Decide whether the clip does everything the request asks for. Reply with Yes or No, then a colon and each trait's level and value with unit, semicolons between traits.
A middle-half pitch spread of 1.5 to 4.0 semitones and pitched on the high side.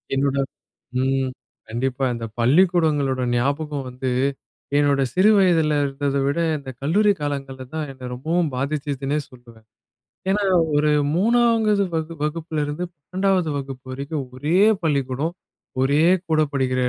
No: average, 3.6 semitones; medium, 145 Hz